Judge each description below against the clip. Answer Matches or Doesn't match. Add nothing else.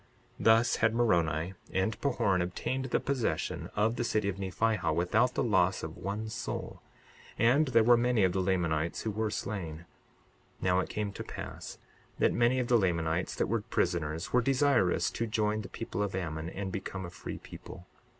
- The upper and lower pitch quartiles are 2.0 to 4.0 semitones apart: Doesn't match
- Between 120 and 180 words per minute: Doesn't match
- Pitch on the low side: Matches